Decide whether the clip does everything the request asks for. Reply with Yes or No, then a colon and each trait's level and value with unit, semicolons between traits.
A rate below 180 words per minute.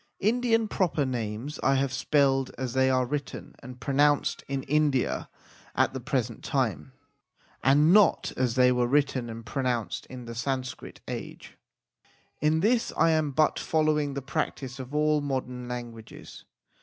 Yes: average, 150 wpm